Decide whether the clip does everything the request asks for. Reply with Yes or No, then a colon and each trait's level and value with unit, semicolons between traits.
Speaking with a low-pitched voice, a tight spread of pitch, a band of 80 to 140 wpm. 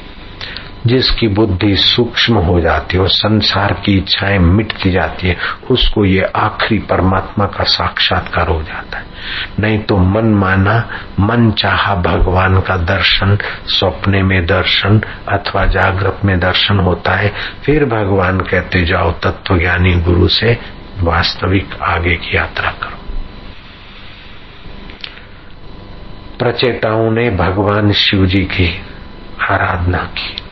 Yes: very low, 95 Hz; narrow, 1.9 semitones; average, 120 wpm